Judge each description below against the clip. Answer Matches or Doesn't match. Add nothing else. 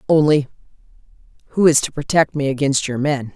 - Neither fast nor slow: Matches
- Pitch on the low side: Doesn't match